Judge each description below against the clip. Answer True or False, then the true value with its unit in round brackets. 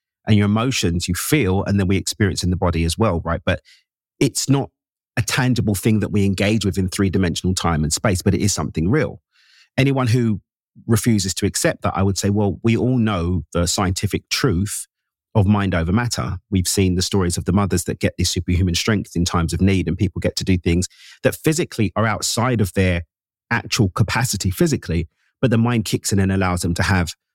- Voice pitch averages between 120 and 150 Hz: False (100 Hz)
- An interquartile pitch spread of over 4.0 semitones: False (3.6 semitones)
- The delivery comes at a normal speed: False (215 wpm)